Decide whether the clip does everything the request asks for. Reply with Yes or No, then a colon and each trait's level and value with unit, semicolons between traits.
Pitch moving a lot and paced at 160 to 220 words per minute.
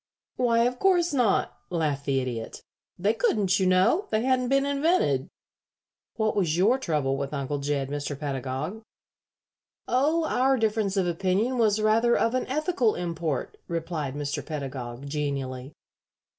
No: wide, 9.0 semitones; average, 145 wpm